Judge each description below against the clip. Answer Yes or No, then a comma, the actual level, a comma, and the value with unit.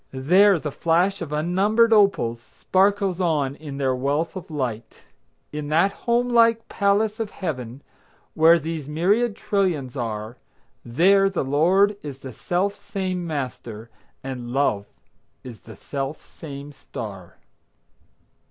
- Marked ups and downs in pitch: Yes, wide, 6.7 semitones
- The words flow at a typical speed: No, slow, 130 wpm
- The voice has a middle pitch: Yes, medium, 160 Hz